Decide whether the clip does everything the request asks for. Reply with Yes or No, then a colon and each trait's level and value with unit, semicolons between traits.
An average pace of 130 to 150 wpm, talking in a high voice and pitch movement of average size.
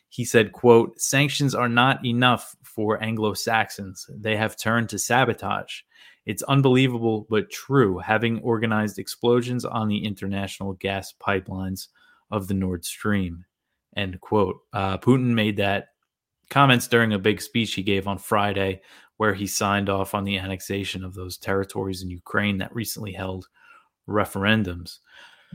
No: average, 145 wpm; low, 105 Hz; average, 3.2 semitones